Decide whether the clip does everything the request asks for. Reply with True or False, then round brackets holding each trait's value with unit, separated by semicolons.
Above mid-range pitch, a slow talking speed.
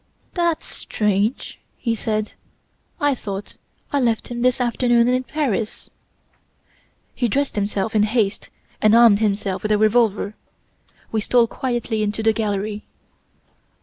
True (220 Hz; 130 wpm)